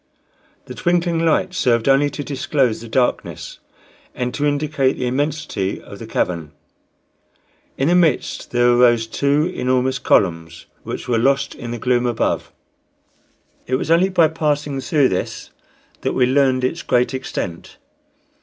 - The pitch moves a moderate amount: Yes, average, 3.4 semitones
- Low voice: Yes, low, 130 Hz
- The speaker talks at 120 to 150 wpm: Yes, average, 145 wpm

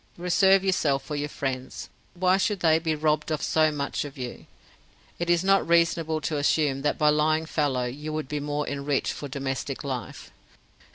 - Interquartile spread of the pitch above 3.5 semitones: No, average, 2.7 semitones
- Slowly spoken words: No, average, 180 wpm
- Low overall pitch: No, medium, 150 Hz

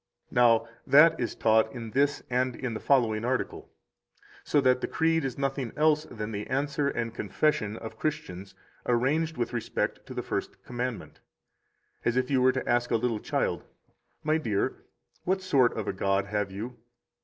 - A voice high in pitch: No, low, 125 Hz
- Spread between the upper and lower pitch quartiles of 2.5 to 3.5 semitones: No, average, 4.0 semitones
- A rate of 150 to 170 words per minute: No, average, 180 wpm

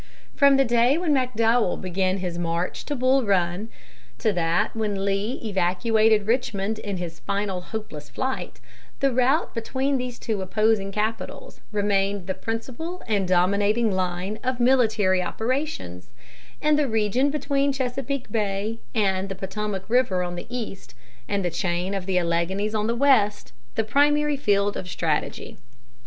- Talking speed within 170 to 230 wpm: No, average, 150 wpm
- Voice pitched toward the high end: Yes, high, 210 Hz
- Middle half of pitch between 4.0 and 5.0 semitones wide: Yes, average, 4.7 semitones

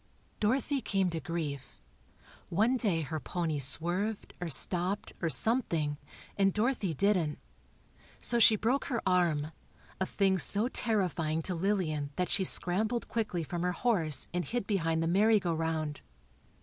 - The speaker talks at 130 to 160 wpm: Yes, average, 150 wpm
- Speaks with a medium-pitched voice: Yes, medium, 180 Hz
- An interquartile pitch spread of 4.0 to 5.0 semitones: Yes, average, 4.5 semitones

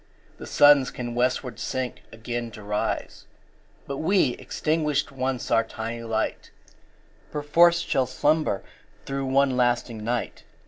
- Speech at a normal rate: No, slow, 130 wpm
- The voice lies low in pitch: Yes, low, 130 Hz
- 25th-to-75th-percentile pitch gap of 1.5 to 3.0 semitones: No, average, 3.7 semitones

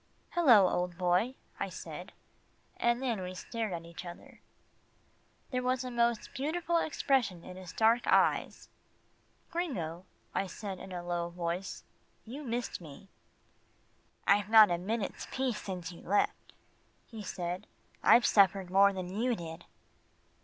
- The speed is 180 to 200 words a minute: No, average, 140 wpm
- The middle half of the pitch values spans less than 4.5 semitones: No, average, 5.1 semitones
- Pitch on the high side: Yes, high, 200 Hz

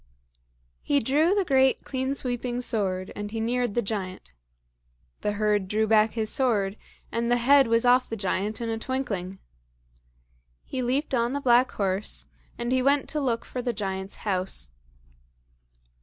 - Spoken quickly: No, average, 160 wpm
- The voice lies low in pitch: No, high, 230 Hz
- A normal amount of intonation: Yes, average, 3.9 semitones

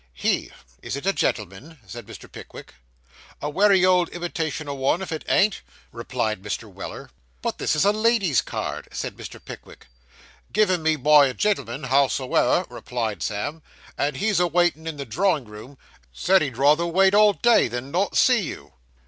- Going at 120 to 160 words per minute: No, average, 175 wpm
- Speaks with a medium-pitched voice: Yes, medium, 155 Hz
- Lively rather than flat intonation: Yes, wide, 6.4 semitones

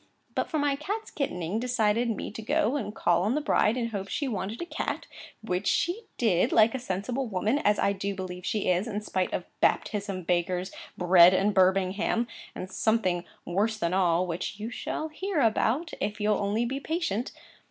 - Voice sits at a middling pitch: No, high, 210 Hz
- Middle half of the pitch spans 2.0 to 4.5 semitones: No, average, 4.9 semitones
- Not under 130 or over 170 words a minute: No, average, 185 wpm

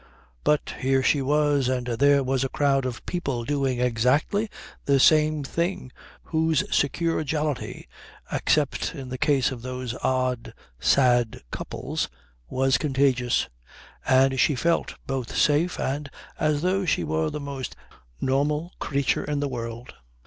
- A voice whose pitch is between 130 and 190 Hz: Yes, low, 135 Hz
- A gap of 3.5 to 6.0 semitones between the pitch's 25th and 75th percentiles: No, average, 2.8 semitones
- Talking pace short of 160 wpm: Yes, average, 140 wpm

